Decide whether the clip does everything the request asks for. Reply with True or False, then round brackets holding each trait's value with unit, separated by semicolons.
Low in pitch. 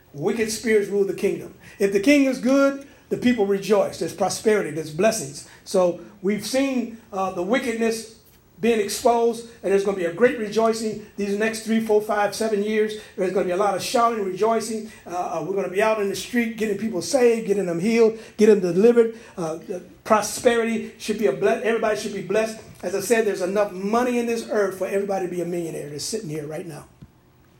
False (210 Hz)